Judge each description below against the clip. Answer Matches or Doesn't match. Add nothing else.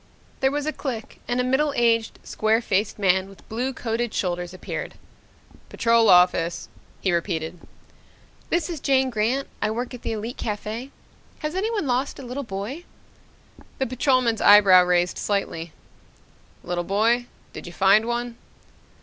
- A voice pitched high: Matches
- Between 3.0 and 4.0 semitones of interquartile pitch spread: Doesn't match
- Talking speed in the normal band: Matches